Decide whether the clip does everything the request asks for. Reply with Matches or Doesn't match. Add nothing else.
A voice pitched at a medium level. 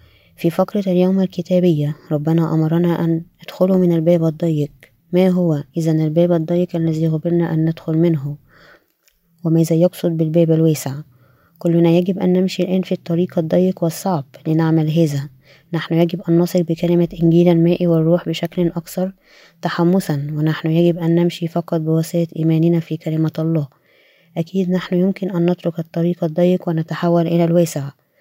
Matches